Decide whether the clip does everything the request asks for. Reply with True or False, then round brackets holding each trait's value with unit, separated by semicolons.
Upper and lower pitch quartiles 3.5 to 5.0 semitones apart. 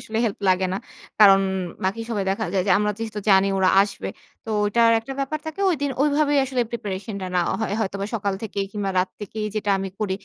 False (2.9 semitones)